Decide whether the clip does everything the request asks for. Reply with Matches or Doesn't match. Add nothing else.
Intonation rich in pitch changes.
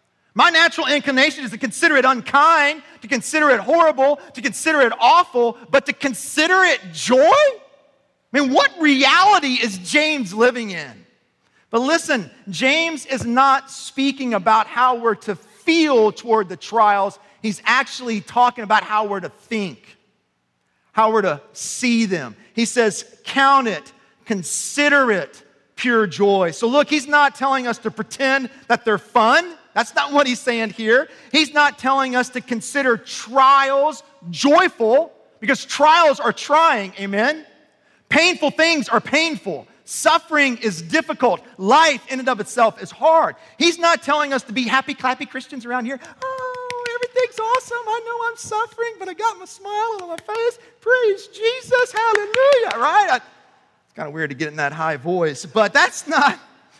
Matches